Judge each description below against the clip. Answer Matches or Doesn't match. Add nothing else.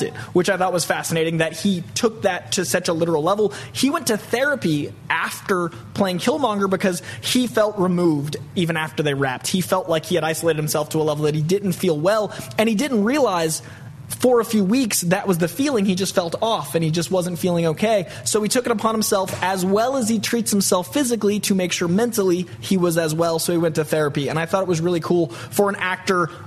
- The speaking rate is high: Matches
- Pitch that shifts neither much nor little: Matches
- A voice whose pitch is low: Doesn't match